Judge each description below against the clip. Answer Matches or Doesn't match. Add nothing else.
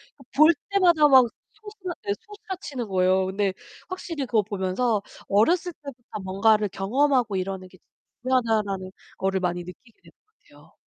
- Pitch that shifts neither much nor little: Doesn't match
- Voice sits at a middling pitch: Doesn't match